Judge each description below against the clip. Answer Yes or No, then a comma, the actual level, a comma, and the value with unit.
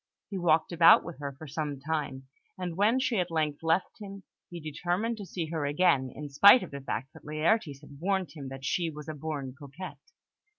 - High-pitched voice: No, medium, 160 Hz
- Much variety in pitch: No, average, 4.2 semitones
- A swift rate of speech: Yes, fast, 210 wpm